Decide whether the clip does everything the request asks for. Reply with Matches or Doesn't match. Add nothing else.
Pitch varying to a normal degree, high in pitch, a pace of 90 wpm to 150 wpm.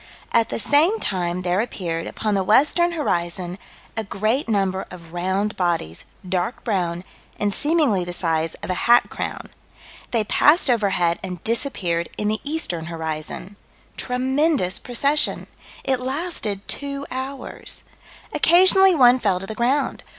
Doesn't match